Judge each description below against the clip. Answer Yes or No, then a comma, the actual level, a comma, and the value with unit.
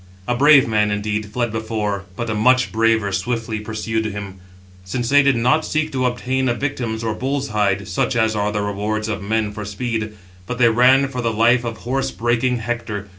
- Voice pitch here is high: No, low, 115 Hz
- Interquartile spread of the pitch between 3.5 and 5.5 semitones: No, average, 2.8 semitones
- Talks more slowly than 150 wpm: No, fast, 205 wpm